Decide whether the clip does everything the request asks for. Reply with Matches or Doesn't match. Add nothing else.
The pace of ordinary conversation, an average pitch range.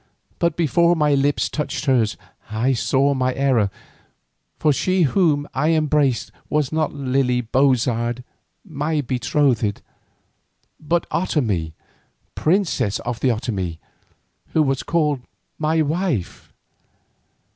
Doesn't match